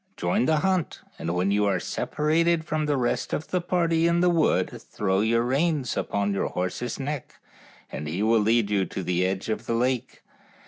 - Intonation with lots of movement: Yes, wide, 8.0 semitones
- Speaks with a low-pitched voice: Yes, low, 120 Hz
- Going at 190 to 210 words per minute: Yes, average, 195 wpm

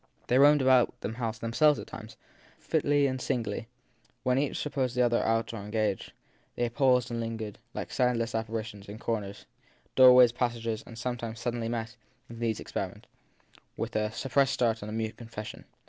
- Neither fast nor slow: Yes, average, 180 wpm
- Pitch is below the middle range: Yes, low, 115 Hz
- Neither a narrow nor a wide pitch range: No, narrow, 2.2 semitones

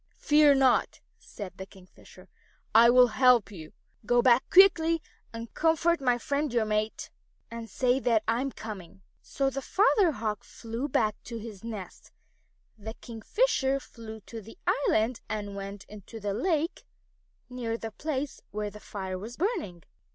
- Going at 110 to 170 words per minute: Yes, average, 160 wpm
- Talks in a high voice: Yes, high, 230 Hz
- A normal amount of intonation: Yes, average, 4.4 semitones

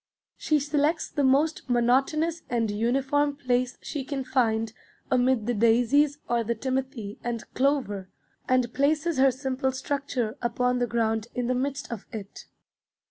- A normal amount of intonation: Yes, average, 3.1 semitones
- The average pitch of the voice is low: No, very high, 255 Hz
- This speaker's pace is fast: No, average, 145 wpm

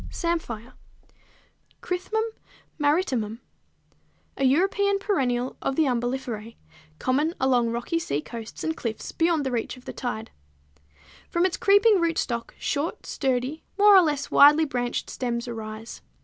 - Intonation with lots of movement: Yes, wide, 5.9 semitones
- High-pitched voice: Yes, very high, 265 Hz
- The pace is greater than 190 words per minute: No, slow, 135 wpm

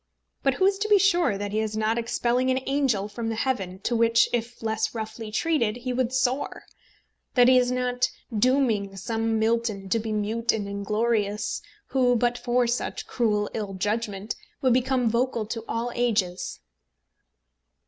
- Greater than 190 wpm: No, average, 170 wpm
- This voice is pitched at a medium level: No, high, 230 Hz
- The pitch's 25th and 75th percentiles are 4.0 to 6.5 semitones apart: No, average, 2.8 semitones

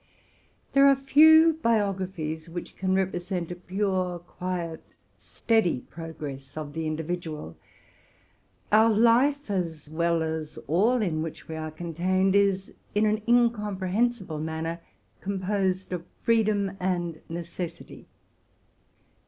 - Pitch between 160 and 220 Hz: Yes, medium, 185 Hz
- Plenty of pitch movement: No, average, 4.3 semitones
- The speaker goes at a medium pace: No, slow, 115 wpm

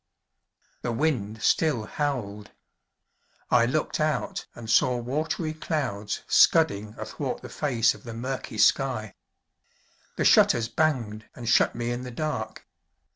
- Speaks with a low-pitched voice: Yes, low, 120 Hz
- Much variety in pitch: No, average, 5.0 semitones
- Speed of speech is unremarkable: No, slow, 130 wpm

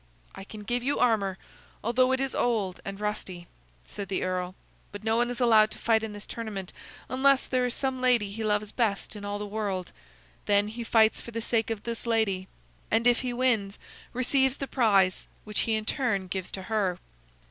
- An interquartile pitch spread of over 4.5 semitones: No, average, 3.3 semitones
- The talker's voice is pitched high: Yes, high, 220 Hz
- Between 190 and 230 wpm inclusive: Yes, average, 200 wpm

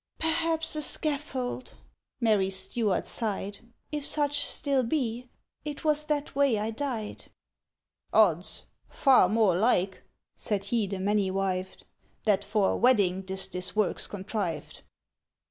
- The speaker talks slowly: Yes, slow, 130 wpm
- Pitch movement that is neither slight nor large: No, wide, 6.4 semitones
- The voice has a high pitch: Yes, high, 220 Hz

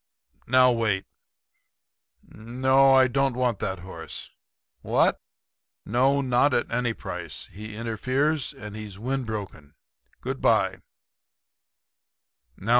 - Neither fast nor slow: No, slow, 95 wpm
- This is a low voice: Yes, low, 120 Hz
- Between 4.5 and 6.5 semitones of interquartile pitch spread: No, average, 3.6 semitones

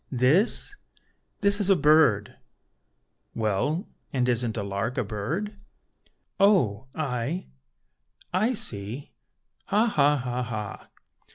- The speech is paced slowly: Yes, slow, 105 wpm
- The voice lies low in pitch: Yes, low, 130 Hz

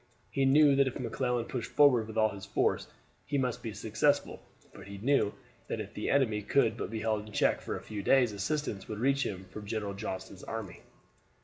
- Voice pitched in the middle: No, low, 110 Hz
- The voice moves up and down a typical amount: Yes, average, 4.5 semitones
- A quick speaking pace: Yes, fast, 215 wpm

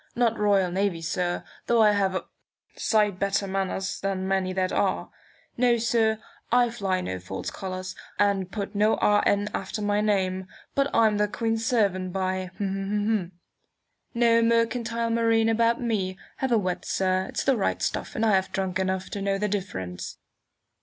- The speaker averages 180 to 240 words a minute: No, average, 165 wpm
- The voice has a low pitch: No, high, 200 Hz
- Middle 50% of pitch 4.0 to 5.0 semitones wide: No, average, 3.1 semitones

